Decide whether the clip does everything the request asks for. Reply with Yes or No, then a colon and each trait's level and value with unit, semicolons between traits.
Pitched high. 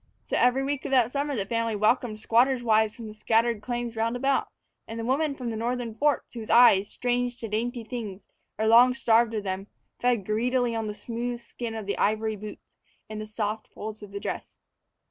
Yes: high, 230 Hz